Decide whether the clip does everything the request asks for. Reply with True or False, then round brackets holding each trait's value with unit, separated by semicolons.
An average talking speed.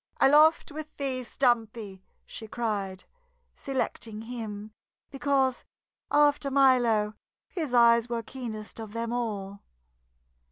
False (105 wpm)